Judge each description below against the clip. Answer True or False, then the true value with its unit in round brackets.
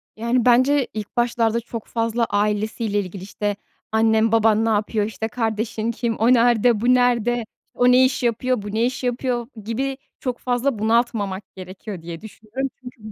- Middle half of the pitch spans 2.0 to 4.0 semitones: True (2.4 semitones)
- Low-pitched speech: False (230 Hz)